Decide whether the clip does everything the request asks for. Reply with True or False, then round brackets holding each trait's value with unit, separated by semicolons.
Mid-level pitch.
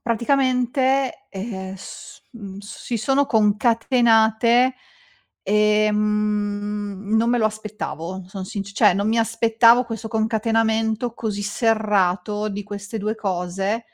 False (215 Hz)